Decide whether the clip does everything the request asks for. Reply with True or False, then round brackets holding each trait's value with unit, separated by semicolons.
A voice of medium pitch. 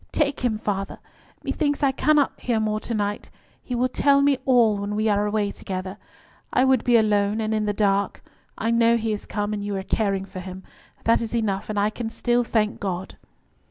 False (215 Hz)